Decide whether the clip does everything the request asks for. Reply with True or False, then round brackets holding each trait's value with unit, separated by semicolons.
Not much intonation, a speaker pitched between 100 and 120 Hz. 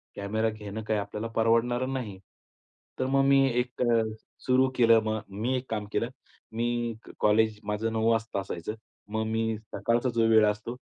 True (1.9 semitones; 110 Hz)